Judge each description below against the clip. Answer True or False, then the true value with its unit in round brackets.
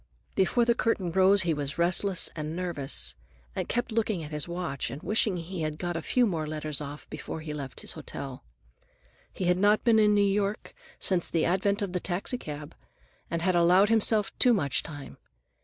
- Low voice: False (175 Hz)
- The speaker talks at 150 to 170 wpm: False (190 wpm)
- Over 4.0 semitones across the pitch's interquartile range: True (4.8 semitones)